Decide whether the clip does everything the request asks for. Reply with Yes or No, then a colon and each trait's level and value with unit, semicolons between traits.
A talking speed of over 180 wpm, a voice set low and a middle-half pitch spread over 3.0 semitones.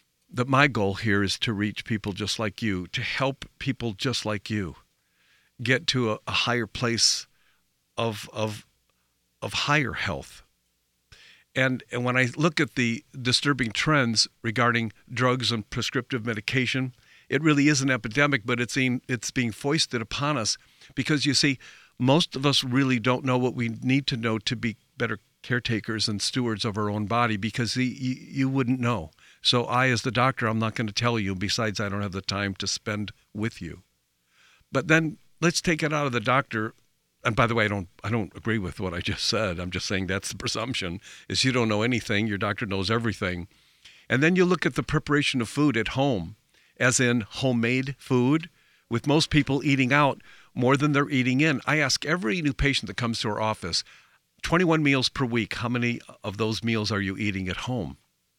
Yes: average, 200 wpm; low, 120 Hz; average, 3.9 semitones